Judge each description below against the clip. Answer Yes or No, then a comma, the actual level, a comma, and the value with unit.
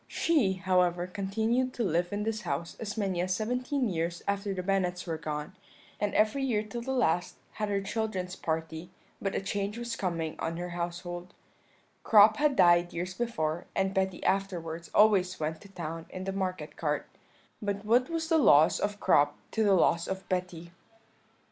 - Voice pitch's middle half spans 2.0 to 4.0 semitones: Yes, average, 3.5 semitones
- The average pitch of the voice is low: No, high, 190 Hz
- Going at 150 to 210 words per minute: Yes, average, 180 wpm